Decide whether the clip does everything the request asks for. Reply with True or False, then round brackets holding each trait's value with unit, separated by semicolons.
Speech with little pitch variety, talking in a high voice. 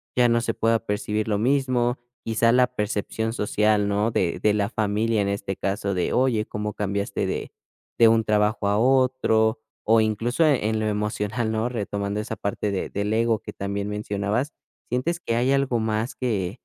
False (2.2 semitones; 110 Hz)